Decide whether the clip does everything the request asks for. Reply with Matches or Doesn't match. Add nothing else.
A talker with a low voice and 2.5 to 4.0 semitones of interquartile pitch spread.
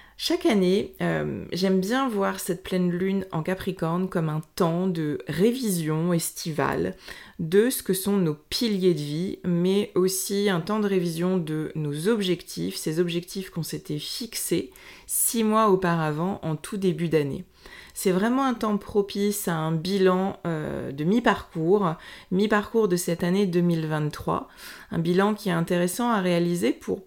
Doesn't match